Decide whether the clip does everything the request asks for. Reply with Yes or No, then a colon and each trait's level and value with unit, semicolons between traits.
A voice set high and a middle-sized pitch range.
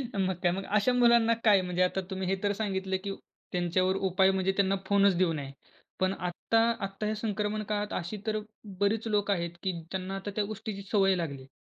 No: high, 195 Hz; narrow, 2.1 semitones